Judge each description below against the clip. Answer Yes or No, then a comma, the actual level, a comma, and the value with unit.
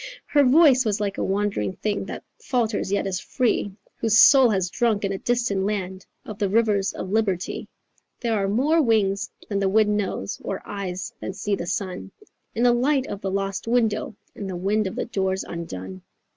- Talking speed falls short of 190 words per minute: No, average, 195 wpm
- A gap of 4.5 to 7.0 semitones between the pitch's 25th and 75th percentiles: No, average, 3.0 semitones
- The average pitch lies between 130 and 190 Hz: No, high, 205 Hz